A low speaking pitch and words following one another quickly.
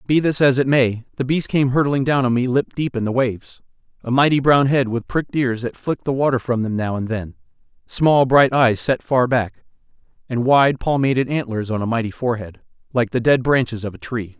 Yes: low, 125 Hz; fast, 225 wpm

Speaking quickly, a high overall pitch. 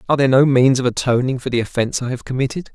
No: fast, 260 wpm; low, 130 Hz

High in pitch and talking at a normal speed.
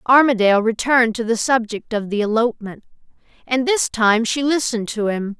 Yes: high, 230 Hz; average, 165 wpm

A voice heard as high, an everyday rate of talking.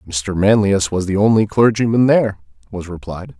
No: low, 100 Hz; average, 160 wpm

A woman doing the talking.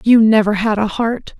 Yes: female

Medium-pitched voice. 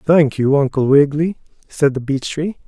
Yes: medium, 145 Hz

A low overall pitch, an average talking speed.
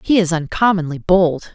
No: medium, 175 Hz; average, 155 wpm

